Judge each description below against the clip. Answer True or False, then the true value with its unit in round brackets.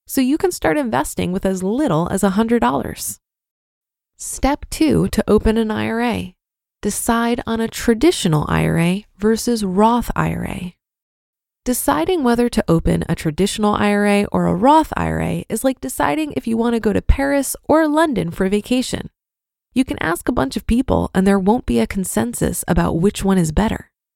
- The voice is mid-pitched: False (215 Hz)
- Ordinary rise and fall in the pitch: True (4.2 semitones)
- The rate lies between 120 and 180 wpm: True (165 wpm)